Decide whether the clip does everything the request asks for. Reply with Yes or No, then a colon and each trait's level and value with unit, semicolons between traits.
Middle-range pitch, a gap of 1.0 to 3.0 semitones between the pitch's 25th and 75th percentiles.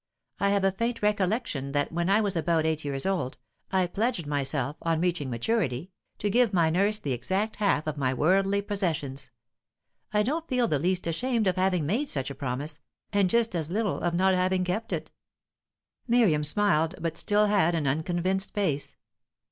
No: medium, 180 Hz; average, 5.2 semitones